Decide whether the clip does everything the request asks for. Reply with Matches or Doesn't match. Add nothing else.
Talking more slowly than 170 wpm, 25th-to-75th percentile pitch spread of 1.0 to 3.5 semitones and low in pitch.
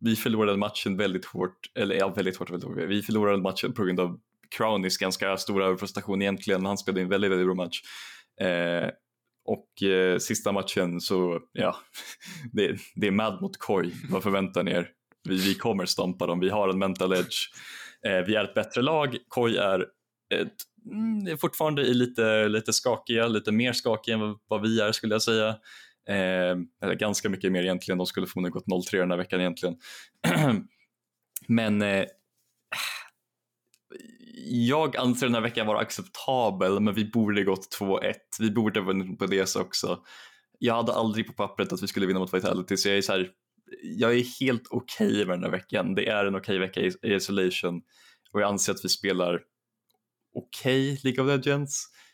Doesn't match